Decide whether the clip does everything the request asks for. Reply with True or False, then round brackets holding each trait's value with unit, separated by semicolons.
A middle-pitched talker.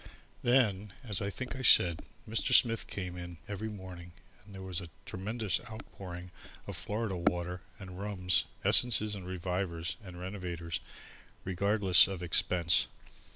False (95 Hz)